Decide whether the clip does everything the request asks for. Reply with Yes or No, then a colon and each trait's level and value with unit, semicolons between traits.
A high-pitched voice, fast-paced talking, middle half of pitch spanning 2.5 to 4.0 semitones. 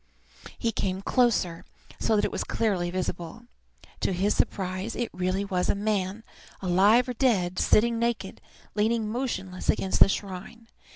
No: high, 200 Hz; average, 150 wpm; average, 3.6 semitones